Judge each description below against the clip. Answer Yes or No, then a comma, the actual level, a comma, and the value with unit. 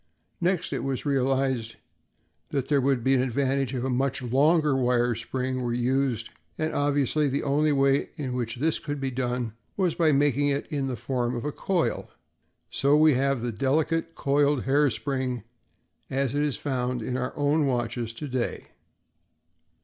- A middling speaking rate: Yes, average, 170 wpm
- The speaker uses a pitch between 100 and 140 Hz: Yes, low, 135 Hz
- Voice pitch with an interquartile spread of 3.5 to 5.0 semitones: No, narrow, 2.5 semitones